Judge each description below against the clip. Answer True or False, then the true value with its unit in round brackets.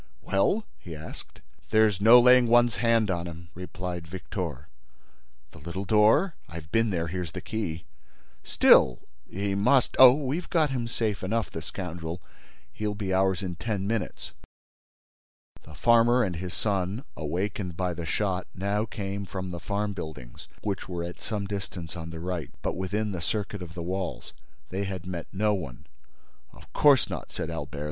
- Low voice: True (95 Hz)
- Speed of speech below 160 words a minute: False (165 wpm)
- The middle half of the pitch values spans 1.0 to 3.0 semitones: False (4.0 semitones)